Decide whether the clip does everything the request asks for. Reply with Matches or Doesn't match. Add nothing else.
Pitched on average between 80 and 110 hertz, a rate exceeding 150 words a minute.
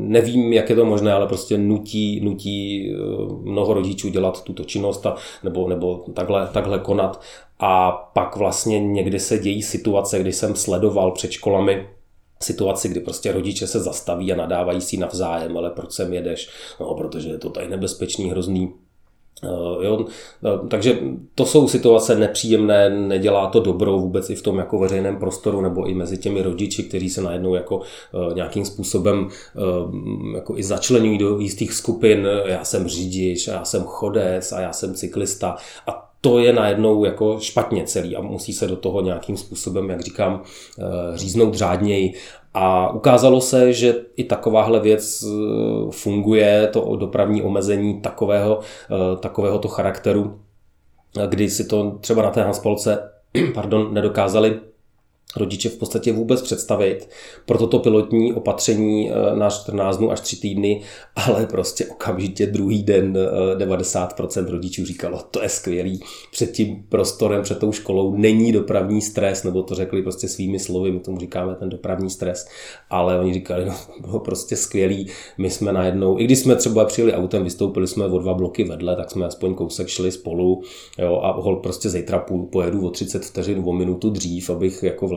Matches